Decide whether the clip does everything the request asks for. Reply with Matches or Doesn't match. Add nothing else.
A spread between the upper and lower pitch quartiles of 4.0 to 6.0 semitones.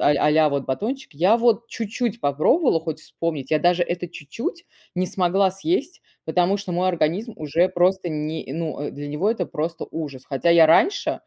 Matches